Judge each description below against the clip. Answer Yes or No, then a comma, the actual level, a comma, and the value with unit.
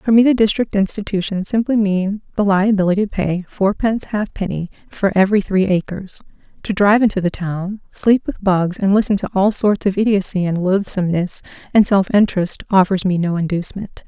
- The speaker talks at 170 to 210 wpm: Yes, average, 175 wpm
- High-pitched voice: Yes, high, 195 Hz